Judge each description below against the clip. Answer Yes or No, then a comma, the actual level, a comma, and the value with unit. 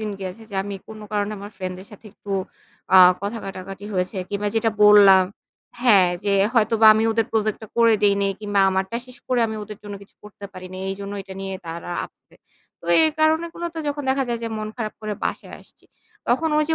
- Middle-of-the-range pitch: No, high, 210 Hz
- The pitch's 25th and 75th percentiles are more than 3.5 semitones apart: No, average, 2.7 semitones